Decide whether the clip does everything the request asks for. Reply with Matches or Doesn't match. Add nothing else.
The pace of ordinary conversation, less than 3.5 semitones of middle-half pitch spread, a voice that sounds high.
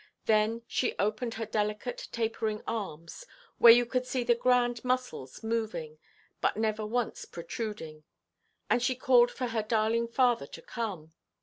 Matches